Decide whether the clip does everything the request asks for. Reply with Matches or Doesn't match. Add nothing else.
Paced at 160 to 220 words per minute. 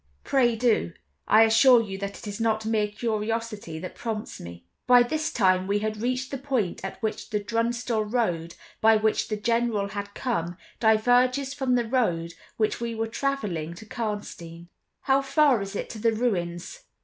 Matches